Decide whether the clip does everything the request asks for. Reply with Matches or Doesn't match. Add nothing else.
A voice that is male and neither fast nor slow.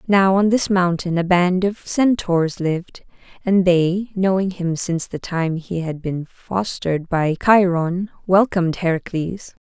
Doesn't match